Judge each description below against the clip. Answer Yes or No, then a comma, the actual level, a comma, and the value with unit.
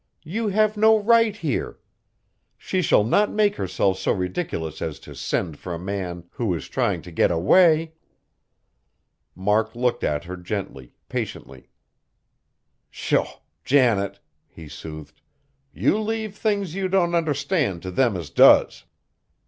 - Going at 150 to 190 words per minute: No, slow, 135 wpm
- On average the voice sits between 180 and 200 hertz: No, low, 120 Hz